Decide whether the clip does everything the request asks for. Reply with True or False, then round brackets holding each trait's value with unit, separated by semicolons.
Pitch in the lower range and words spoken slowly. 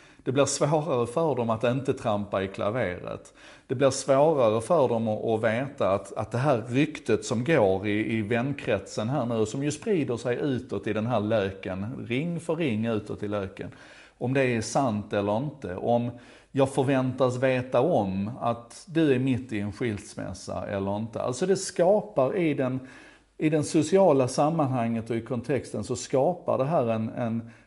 False (125 Hz; 175 wpm)